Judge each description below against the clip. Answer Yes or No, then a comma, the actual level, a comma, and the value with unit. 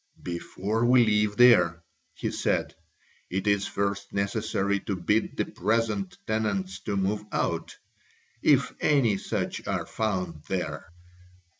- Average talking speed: No, slow, 125 wpm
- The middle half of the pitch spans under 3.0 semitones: Yes, narrow, 2.5 semitones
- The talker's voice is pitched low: Yes, low, 100 Hz